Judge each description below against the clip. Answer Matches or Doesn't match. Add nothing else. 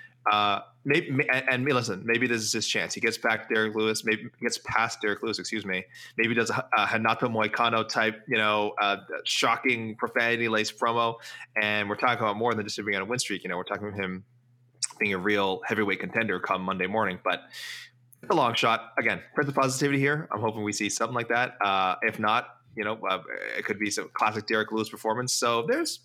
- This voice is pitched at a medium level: Doesn't match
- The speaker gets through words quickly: Matches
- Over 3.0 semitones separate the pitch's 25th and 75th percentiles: Doesn't match